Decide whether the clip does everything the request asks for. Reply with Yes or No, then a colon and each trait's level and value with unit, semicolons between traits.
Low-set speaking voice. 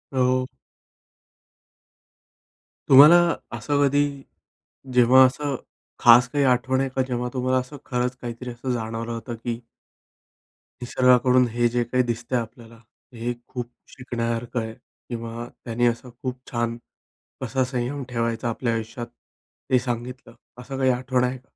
Yes: low, 125 Hz